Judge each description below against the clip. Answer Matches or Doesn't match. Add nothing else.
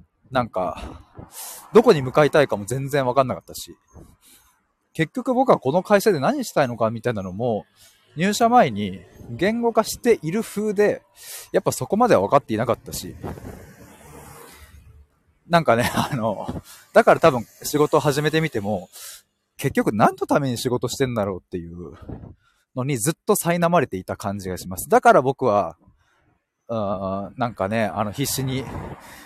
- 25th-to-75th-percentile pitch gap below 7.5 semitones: Doesn't match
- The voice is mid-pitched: Doesn't match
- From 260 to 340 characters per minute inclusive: Matches